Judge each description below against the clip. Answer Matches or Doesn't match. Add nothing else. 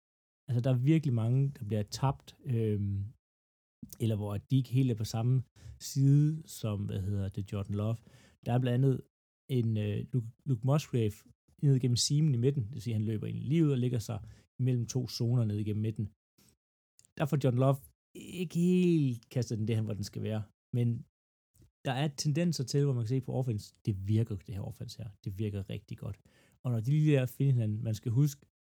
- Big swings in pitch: Doesn't match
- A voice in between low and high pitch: Doesn't match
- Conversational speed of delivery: Matches